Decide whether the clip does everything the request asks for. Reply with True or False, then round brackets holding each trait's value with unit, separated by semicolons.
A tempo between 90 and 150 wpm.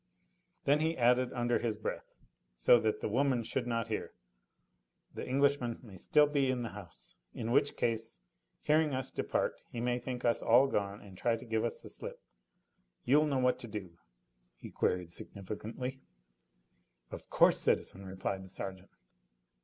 False (165 wpm)